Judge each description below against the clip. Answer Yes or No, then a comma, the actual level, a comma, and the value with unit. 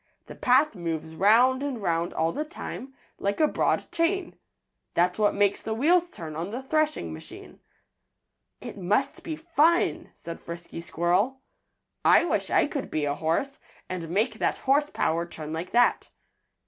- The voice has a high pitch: Yes, high, 210 Hz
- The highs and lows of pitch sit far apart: Yes, wide, 8.9 semitones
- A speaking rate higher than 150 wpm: Yes, average, 160 wpm